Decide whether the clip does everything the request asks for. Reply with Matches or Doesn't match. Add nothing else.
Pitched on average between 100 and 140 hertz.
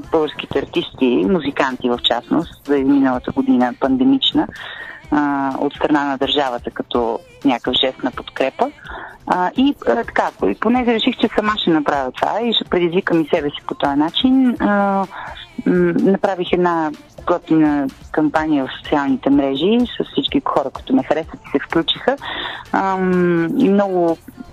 Doesn't match